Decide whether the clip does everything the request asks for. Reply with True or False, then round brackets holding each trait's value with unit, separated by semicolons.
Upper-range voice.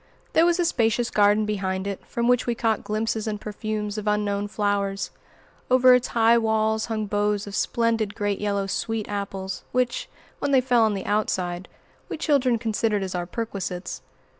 True (215 Hz)